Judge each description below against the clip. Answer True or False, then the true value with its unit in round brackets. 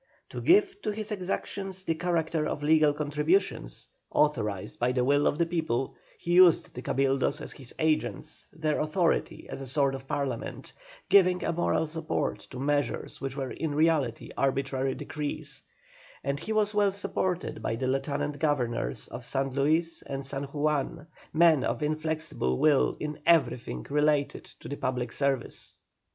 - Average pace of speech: True (160 wpm)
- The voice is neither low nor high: True (150 Hz)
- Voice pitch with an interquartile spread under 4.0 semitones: True (3.3 semitones)